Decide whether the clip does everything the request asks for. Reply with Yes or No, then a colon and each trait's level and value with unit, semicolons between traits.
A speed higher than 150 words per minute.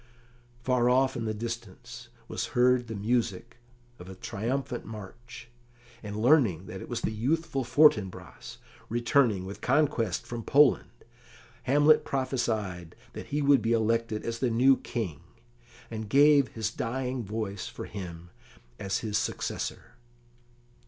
No: slow, 135 wpm